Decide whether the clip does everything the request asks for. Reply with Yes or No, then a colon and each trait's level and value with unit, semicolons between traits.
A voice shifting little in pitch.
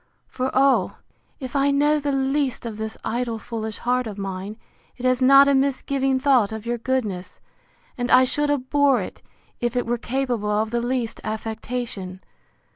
No: average, 3.5 semitones